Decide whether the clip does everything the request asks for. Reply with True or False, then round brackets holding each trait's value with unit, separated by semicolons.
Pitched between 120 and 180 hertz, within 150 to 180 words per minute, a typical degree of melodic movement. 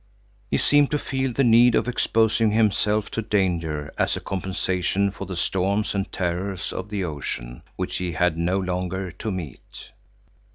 False (95 Hz; 165 wpm; 3.3 semitones)